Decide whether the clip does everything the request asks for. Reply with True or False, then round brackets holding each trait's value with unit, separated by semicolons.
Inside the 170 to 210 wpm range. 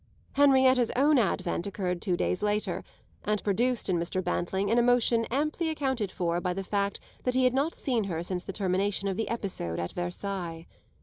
True (185 wpm)